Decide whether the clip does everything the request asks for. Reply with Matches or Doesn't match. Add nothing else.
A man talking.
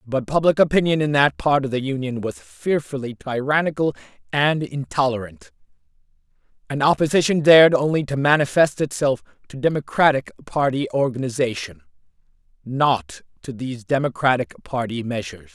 Matches